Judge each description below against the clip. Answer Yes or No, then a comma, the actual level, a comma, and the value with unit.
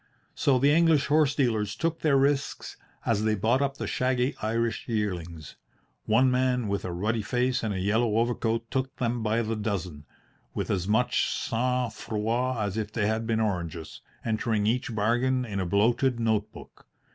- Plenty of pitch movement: No, average, 3.2 semitones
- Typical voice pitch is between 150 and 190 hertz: No, low, 115 Hz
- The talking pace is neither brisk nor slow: Yes, average, 175 wpm